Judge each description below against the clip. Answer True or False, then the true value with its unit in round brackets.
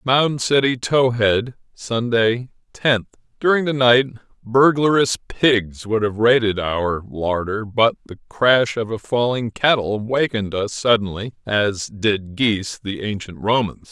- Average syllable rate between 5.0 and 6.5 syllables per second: False (4.0 syllables/s)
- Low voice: True (115 Hz)